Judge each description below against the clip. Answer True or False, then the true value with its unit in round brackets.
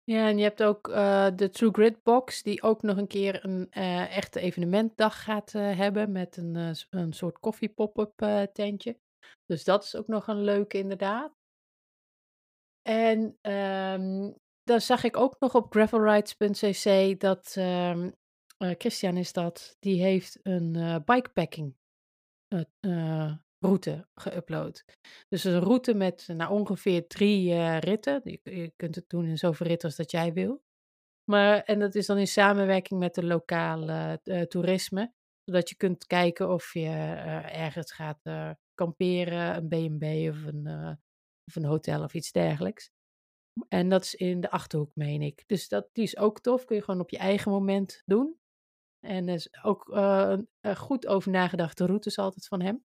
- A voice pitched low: False (190 Hz)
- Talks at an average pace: True (170 wpm)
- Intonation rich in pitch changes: False (3.4 semitones)